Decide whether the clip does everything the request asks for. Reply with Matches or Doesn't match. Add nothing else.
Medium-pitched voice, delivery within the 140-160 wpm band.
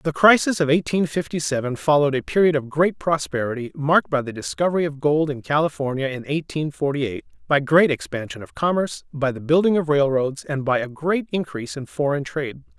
Doesn't match